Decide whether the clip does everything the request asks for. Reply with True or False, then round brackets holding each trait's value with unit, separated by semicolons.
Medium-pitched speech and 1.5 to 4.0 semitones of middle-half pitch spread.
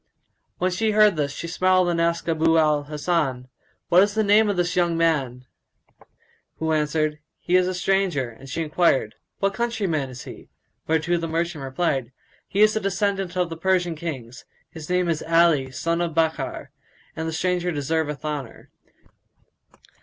True (165 Hz; 3.2 semitones)